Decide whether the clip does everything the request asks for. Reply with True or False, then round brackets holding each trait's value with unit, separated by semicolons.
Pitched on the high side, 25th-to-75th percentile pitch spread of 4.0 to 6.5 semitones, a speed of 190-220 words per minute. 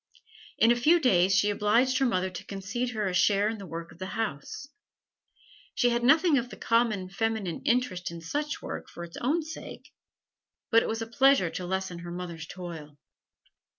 True (205 Hz; 5.1 semitones; 195 wpm)